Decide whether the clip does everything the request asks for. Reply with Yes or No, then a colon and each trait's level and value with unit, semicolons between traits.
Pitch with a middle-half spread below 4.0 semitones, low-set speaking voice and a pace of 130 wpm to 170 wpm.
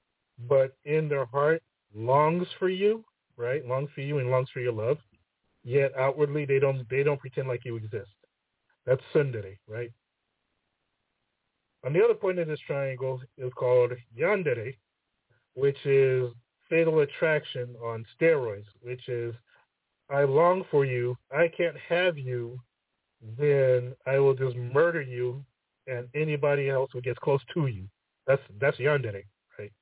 Yes: average, 3.3 semitones; low, 130 Hz; average, 145 wpm